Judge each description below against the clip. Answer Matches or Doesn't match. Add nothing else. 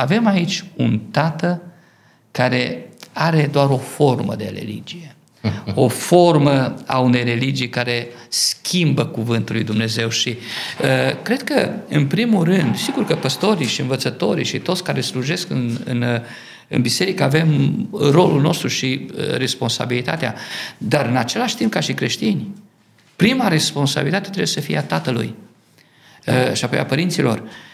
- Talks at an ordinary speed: Matches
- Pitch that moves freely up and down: Matches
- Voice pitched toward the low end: Doesn't match